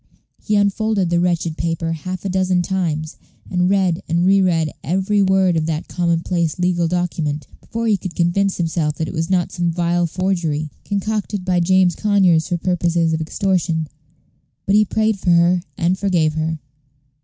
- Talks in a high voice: No, medium, 175 Hz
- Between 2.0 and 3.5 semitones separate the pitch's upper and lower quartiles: Yes, narrow, 2.4 semitones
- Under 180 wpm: Yes, average, 165 wpm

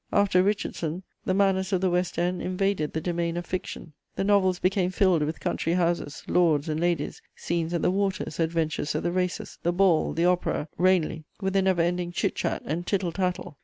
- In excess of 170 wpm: Yes, average, 200 wpm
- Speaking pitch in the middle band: Yes, medium, 175 Hz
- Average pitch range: No, narrow, 2.0 semitones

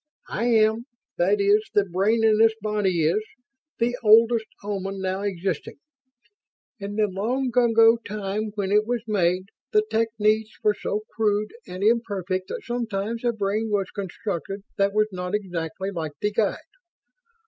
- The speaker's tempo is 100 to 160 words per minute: Yes, average, 150 wpm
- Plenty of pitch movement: No, narrow, 2.4 semitones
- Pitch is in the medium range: No, high, 210 Hz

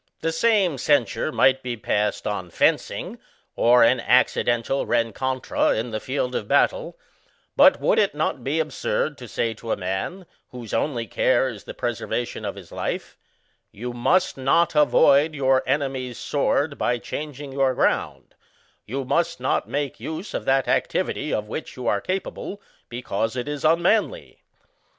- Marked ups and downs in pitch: No, average, 4.0 semitones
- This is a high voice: No, low, 130 Hz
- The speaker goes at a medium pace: Yes, average, 160 wpm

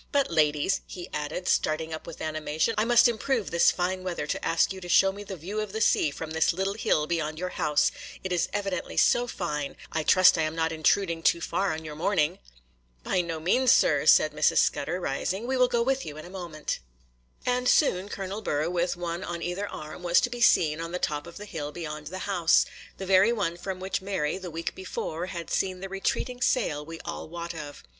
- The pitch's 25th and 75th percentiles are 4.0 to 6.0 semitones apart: No, average, 3.6 semitones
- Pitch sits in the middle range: Yes, medium, 175 Hz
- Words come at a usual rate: No, fast, 220 wpm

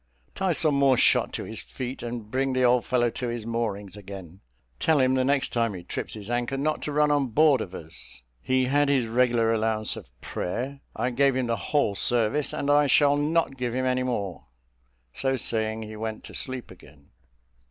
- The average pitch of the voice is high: No, low, 125 Hz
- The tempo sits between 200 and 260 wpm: Yes, fast, 205 wpm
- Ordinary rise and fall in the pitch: Yes, average, 3.5 semitones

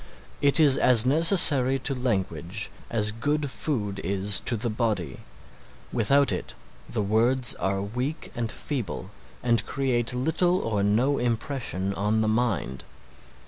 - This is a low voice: Yes, low, 120 Hz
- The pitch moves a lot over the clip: No, average, 4.6 semitones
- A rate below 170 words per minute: Yes, slow, 135 wpm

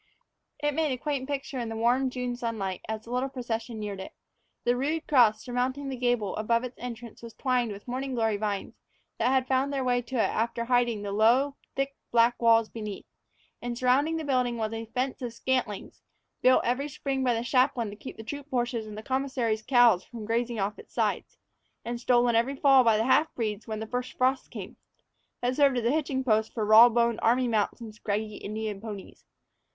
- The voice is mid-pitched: No, high, 240 Hz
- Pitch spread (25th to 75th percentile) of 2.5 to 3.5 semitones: Yes, average, 2.8 semitones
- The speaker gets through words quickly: Yes, fast, 210 wpm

